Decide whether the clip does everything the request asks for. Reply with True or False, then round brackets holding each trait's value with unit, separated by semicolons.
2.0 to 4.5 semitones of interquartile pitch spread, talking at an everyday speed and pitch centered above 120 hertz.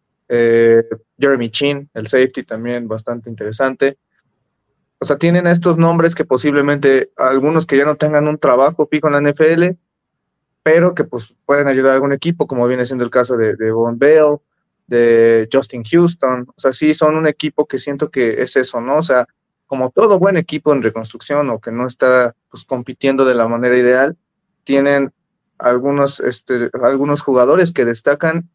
True (3.7 semitones; 175 wpm; 140 Hz)